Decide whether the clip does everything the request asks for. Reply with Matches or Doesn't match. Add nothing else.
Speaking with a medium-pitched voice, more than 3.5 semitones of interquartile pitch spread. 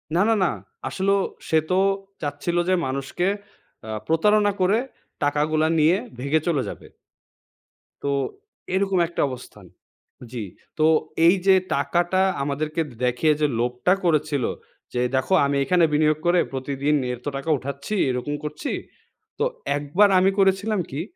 Matches